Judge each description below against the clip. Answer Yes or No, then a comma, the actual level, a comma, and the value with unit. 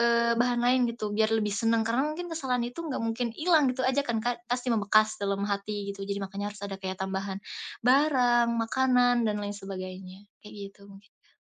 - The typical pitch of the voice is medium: No, high, 225 Hz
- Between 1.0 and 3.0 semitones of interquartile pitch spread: No, average, 3.5 semitones